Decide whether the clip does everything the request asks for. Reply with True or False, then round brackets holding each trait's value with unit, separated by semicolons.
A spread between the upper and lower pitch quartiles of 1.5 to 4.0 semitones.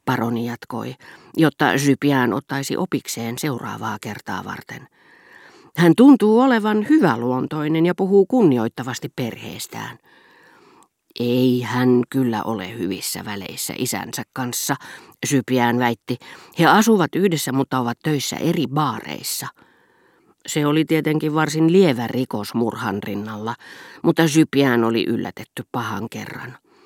False (5.0 semitones)